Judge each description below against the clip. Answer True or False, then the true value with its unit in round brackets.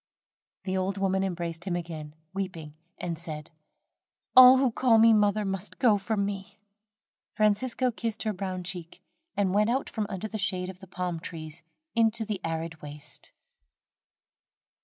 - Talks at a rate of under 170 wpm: True (155 wpm)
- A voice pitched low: False (190 Hz)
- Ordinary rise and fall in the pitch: True (3.9 semitones)